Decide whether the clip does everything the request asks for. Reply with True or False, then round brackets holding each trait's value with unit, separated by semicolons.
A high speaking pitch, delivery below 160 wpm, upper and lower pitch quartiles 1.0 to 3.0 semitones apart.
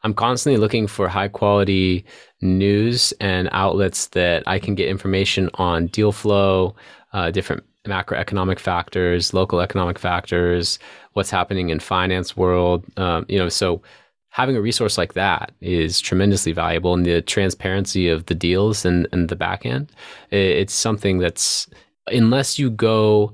False (95 Hz; 150 wpm; 2.5 semitones)